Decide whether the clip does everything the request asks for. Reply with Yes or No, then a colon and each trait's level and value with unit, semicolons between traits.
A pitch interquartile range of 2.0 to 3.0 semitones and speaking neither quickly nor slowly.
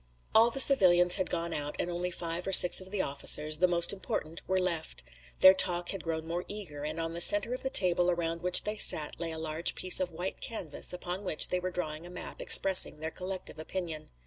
No: narrow, 2.4 semitones; fast, 225 wpm